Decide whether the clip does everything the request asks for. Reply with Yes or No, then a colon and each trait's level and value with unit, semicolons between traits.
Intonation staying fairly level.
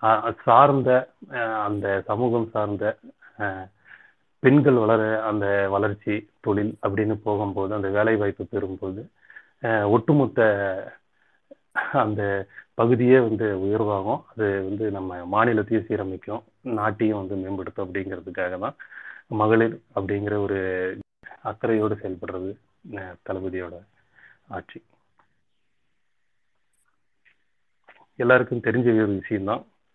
Yes: narrow, 2.2 semitones